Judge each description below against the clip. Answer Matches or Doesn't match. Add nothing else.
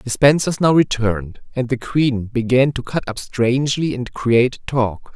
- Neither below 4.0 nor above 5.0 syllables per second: Matches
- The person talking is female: Doesn't match